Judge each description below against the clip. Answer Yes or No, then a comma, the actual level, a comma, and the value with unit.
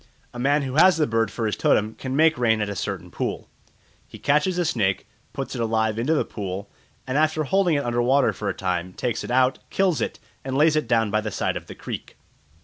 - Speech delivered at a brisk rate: Yes, fast, 235 wpm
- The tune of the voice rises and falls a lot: Yes, wide, 5.8 semitones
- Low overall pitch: Yes, low, 125 Hz